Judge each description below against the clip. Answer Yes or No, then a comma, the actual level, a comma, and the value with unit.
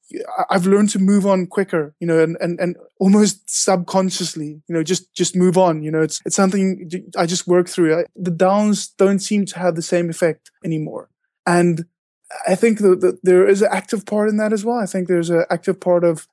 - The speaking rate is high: Yes, fast, 220 wpm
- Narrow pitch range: Yes, narrow, 2.2 semitones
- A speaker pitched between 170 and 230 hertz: Yes, medium, 185 Hz